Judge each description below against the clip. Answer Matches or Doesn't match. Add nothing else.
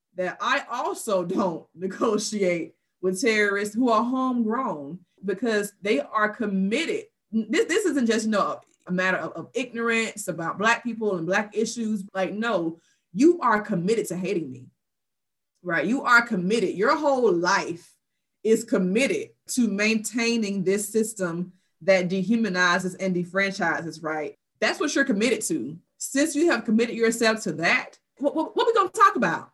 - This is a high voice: Matches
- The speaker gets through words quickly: Doesn't match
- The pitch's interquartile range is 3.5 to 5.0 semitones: Matches